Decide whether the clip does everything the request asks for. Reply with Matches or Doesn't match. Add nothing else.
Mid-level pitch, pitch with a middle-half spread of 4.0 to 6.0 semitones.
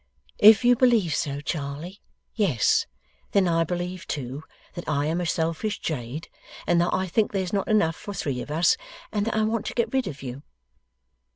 Matches